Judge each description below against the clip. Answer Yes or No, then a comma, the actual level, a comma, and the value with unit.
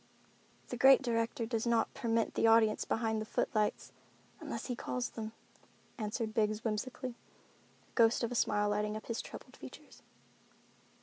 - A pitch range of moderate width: No, narrow, 1.6 semitones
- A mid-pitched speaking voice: No, high, 225 Hz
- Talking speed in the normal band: Yes, average, 150 wpm